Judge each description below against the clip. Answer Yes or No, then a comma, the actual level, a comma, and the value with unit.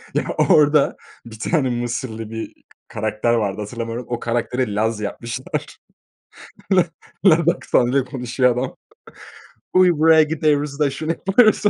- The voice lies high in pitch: No, low, 125 Hz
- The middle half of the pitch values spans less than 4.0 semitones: No, average, 4.9 semitones